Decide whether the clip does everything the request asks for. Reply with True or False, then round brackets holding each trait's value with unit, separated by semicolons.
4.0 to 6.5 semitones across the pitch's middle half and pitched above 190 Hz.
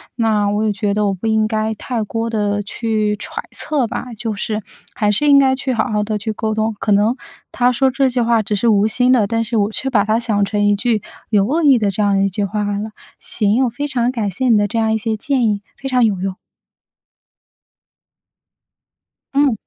False (2.8 semitones; 220 Hz)